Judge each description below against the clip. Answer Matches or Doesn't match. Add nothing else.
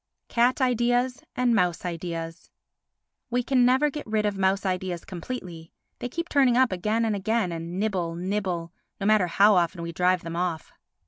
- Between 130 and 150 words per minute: Doesn't match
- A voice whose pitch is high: Matches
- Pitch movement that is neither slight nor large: Doesn't match